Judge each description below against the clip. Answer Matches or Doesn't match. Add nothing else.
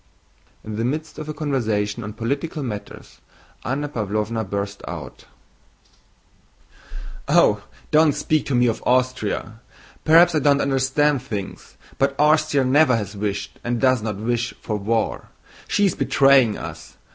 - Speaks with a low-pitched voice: Matches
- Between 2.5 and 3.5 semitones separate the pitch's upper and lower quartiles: Doesn't match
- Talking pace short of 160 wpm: Matches